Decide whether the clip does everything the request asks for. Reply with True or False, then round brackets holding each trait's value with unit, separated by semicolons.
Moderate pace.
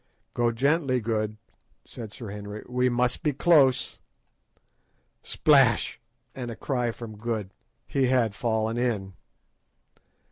False (115 wpm)